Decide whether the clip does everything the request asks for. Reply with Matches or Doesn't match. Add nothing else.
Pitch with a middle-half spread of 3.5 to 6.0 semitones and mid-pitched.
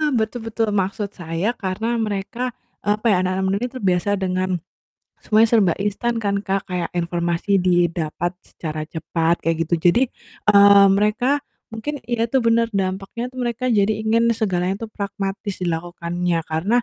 Doesn't match